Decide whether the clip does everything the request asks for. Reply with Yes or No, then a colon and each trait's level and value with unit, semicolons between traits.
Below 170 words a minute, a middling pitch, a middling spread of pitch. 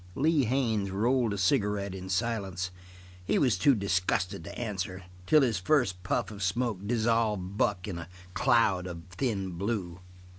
No: average, 155 wpm; low, 100 Hz; average, 4.1 semitones